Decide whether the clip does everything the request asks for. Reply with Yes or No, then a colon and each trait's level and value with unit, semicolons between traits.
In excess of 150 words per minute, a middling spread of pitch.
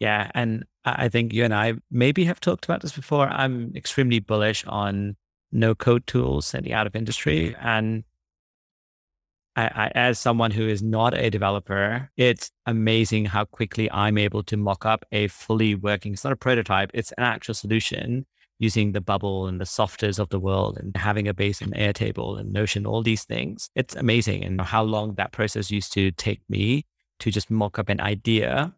No: average, 190 wpm; narrow, 2.3 semitones